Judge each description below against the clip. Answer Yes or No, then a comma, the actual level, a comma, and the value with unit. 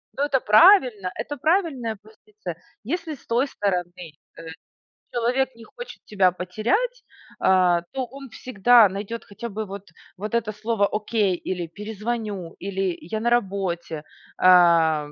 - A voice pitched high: Yes, high, 215 Hz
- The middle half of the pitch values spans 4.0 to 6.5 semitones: Yes, average, 4.7 semitones